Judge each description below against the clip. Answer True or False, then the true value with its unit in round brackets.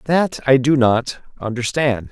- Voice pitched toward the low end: True (130 Hz)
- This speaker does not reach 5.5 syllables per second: True (4.1 syllables/s)